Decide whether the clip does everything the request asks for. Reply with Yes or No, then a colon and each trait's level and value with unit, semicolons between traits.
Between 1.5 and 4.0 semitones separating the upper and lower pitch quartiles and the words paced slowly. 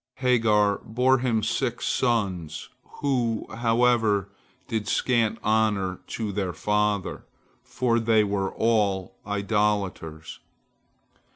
Yes: narrow, 2.6 semitones; slow, 95 wpm